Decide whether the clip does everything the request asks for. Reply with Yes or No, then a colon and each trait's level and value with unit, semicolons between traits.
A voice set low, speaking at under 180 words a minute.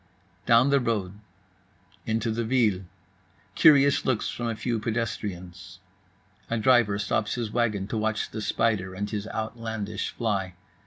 Yes: low, 110 Hz; average, 140 wpm